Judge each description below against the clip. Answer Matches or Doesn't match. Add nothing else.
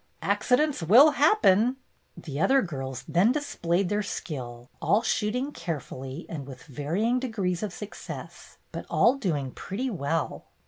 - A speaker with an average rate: Matches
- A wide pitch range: Matches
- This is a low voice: Doesn't match